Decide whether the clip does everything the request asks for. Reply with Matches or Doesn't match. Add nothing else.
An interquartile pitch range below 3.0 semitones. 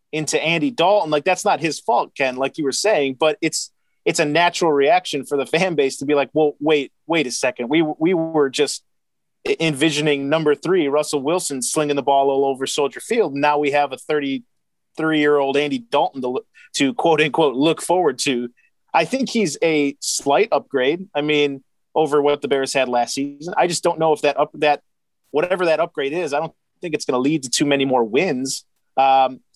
Matches